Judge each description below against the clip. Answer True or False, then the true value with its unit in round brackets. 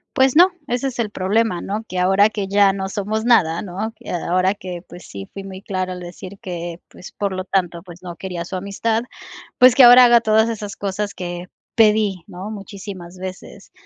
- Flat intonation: False (3.2 semitones)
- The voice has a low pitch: False (195 Hz)